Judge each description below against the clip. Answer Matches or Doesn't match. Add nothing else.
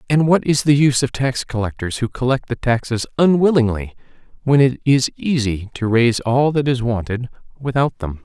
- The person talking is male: Matches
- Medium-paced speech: Matches